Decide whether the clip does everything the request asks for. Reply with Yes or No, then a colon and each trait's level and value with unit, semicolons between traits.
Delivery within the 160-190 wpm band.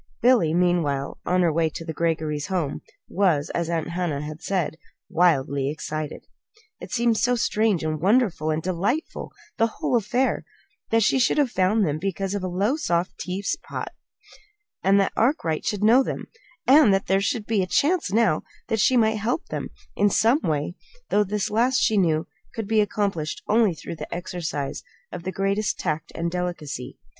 Yes: average, 170 wpm